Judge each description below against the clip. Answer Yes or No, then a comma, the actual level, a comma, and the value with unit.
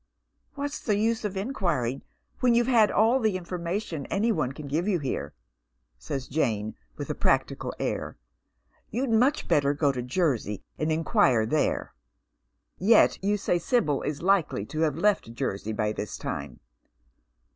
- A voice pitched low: No, medium, 165 Hz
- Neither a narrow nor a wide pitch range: No, wide, 8.4 semitones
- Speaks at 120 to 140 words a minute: No, average, 165 wpm